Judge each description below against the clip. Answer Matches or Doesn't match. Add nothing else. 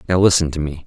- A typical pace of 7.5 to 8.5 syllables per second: Doesn't match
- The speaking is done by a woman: Doesn't match